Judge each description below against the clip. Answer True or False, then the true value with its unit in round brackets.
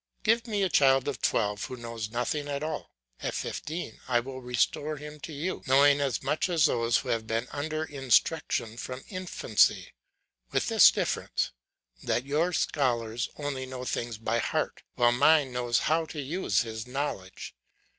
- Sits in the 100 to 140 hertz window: True (135 Hz)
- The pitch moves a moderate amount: True (4.2 semitones)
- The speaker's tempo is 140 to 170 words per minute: True (165 wpm)